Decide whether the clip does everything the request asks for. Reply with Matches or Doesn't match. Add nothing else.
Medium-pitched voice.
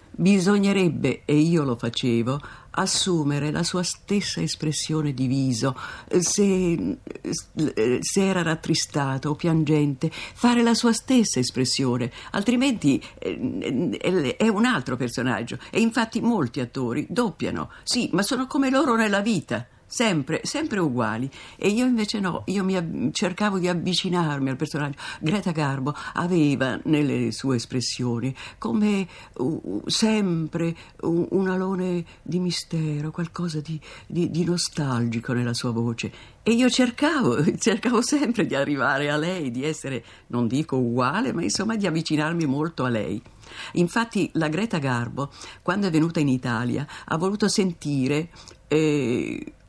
Matches